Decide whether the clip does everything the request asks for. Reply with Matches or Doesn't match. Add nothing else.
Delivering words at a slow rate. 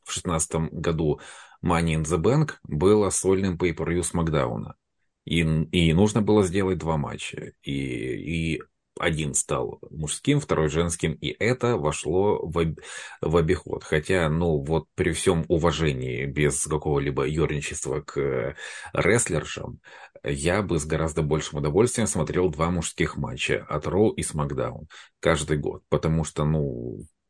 Doesn't match